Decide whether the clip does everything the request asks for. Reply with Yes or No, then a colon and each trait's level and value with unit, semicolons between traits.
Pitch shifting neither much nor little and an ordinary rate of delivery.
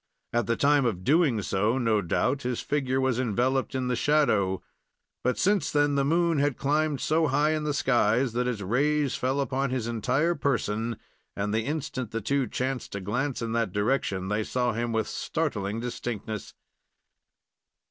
Yes: average, 4.1 semitones; average, 175 wpm